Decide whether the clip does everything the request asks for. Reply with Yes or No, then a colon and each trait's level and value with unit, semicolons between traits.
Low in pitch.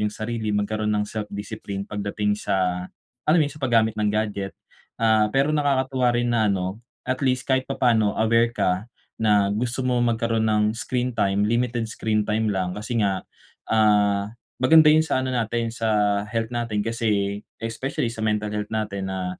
Yes: low, 110 Hz